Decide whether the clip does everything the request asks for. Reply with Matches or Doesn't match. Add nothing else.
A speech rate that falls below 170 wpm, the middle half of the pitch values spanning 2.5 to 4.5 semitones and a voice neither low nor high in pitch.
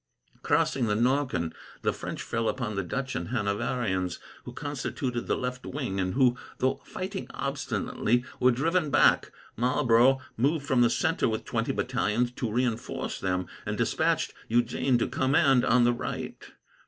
Doesn't match